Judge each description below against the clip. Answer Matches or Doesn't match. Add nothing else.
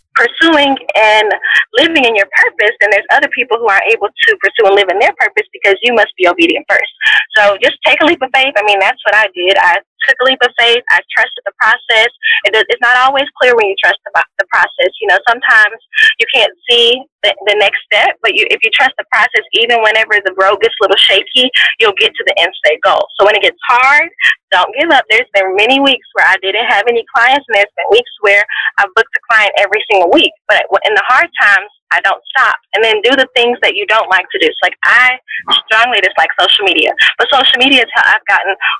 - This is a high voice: Matches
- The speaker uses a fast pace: Matches